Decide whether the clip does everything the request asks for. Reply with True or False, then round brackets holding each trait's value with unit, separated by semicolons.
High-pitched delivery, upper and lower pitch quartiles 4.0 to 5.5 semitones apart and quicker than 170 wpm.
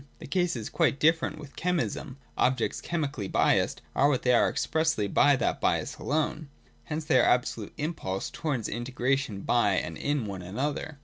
False (135 Hz; 4.8 semitones; 180 wpm)